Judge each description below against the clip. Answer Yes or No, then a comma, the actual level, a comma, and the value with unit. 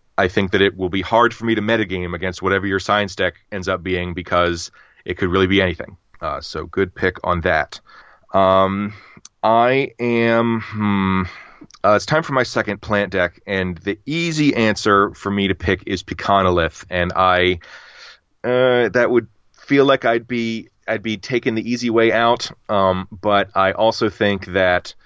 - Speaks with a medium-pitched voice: No, low, 100 Hz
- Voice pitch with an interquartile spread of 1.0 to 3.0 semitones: No, average, 3.5 semitones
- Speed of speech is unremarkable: Yes, average, 180 wpm